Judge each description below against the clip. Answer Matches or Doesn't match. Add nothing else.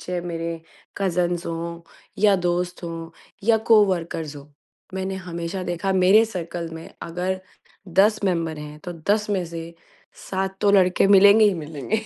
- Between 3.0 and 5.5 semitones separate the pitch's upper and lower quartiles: Doesn't match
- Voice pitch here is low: Doesn't match